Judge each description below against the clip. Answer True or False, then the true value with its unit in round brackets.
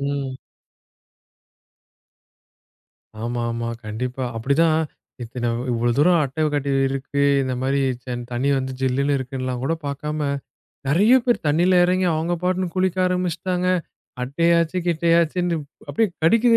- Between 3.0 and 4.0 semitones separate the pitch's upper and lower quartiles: False (5.0 semitones)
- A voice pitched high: False (150 Hz)